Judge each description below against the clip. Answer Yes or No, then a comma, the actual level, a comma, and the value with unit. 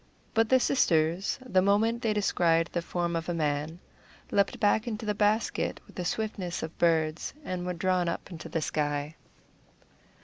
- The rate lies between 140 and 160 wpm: No, average, 170 wpm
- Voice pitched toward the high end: No, medium, 180 Hz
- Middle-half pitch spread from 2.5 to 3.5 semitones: No, average, 4.2 semitones